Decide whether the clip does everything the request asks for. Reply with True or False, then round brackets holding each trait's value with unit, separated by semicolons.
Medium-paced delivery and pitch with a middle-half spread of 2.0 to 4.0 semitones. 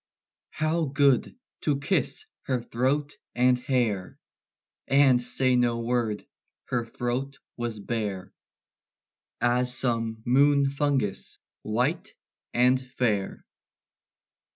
False (95 wpm; 2.8 semitones)